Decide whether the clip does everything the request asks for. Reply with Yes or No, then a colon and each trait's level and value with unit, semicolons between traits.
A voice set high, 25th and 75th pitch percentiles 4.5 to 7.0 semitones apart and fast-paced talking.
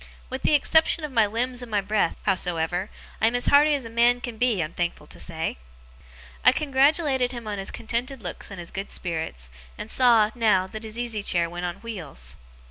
Yes: high, 220 Hz; wide, 5.5 semitones; fast, 210 wpm